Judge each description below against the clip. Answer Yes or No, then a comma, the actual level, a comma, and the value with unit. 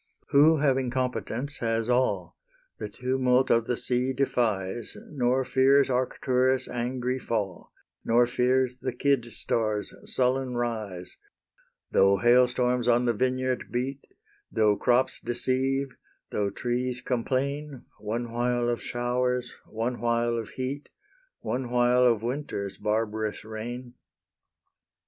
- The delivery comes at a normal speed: No, slow, 120 wpm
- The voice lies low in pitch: Yes, low, 125 Hz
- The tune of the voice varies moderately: No, narrow, 1.7 semitones